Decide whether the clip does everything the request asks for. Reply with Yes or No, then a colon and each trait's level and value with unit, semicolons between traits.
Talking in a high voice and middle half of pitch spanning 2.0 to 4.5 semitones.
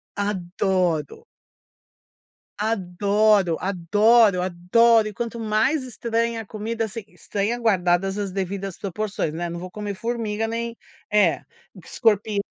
Yes: high, 210 Hz; average, 3.3 semitones